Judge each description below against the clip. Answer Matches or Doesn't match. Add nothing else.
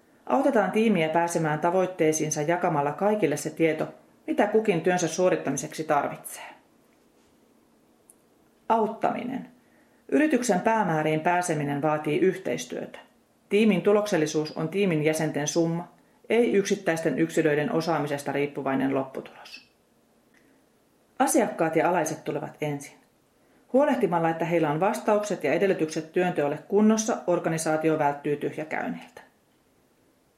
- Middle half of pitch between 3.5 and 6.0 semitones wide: Matches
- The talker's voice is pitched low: Doesn't match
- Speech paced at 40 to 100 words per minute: Matches